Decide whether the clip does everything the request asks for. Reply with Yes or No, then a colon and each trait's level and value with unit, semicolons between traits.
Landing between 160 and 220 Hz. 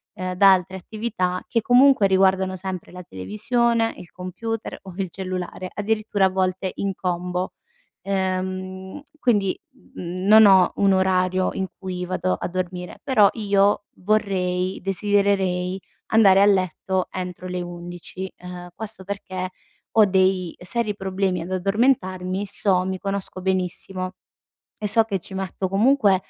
Yes: high, 190 Hz